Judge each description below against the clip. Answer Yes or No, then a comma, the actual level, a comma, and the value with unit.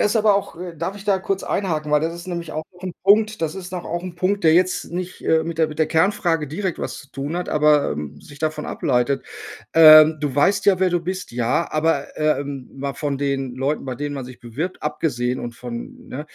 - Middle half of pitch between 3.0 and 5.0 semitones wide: Yes, average, 4.2 semitones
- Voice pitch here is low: No, medium, 155 Hz